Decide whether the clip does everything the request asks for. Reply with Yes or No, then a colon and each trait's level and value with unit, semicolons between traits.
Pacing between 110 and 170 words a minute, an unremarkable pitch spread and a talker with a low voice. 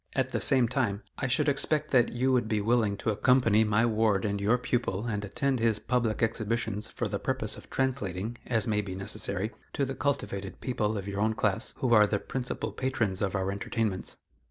No: fast, 205 wpm; average, 3.5 semitones; low, 110 Hz